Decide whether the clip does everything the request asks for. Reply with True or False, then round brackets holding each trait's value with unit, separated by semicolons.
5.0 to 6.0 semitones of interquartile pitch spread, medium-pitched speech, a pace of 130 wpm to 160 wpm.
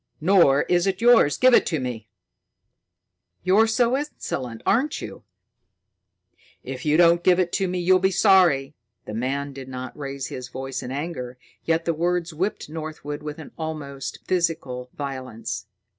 True (5.3 semitones; 155 Hz; 155 wpm)